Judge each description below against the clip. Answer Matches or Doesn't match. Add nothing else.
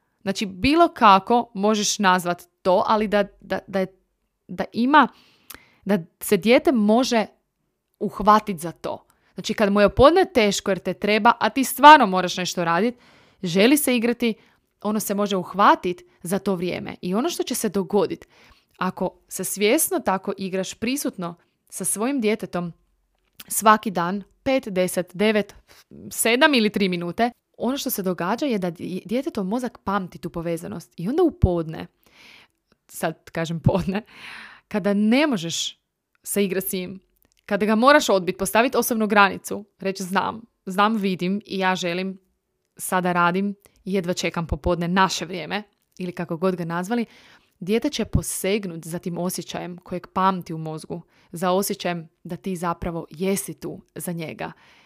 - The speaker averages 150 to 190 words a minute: Matches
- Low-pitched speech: Doesn't match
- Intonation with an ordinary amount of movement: Matches